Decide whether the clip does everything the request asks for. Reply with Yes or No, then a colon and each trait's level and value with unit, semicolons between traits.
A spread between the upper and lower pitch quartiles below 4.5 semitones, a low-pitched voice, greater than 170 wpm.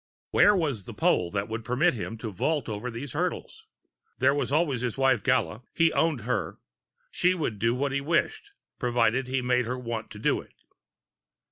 Yes: average, 3.9 semitones; low, 125 Hz; average, 190 wpm